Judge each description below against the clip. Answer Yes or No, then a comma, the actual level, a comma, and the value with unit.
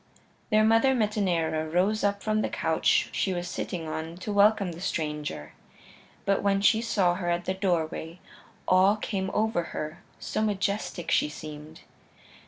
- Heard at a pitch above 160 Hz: Yes, medium, 185 Hz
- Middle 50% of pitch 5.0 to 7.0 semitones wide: No, average, 4.2 semitones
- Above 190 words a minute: No, average, 155 wpm